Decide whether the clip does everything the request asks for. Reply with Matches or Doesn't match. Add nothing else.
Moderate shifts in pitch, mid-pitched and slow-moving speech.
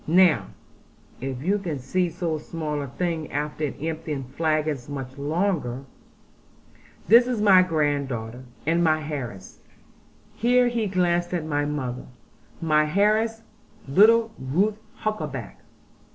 Matches